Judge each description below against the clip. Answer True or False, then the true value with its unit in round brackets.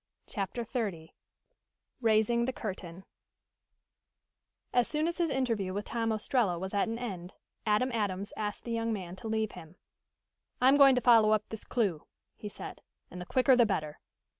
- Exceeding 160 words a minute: True (170 wpm)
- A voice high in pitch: True (220 Hz)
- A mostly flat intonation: False (4.0 semitones)